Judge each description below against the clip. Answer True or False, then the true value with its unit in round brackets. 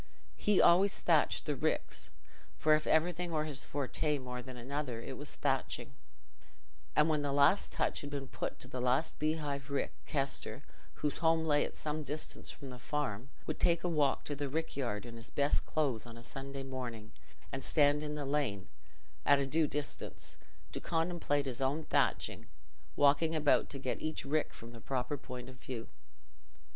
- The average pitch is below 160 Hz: True (140 Hz)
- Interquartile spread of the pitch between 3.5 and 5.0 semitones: False (3.0 semitones)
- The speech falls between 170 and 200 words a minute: True (180 wpm)